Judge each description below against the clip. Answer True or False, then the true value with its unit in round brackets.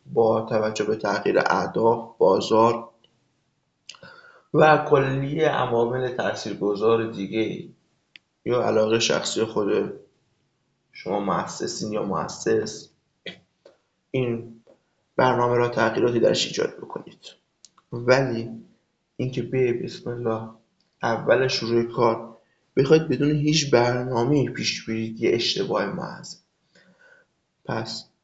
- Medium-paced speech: False (95 wpm)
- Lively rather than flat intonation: False (2.9 semitones)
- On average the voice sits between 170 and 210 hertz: False (120 Hz)